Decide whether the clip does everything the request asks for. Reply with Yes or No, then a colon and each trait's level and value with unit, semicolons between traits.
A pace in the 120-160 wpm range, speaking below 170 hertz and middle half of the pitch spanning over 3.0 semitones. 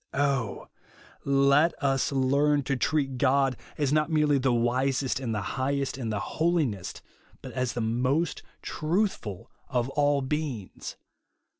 No: slow, 135 wpm; low, 135 Hz; average, 2.7 semitones